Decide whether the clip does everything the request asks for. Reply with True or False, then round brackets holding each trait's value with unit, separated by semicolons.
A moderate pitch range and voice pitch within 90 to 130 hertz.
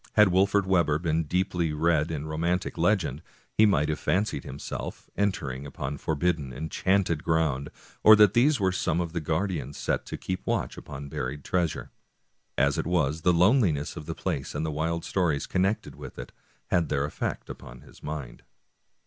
False (4.0 semitones; 80 Hz)